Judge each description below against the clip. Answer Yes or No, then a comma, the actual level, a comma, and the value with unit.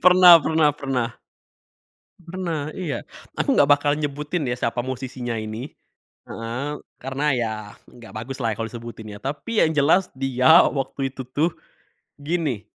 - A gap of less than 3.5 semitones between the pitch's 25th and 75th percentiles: No, average, 4.5 semitones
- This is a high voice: No, low, 135 Hz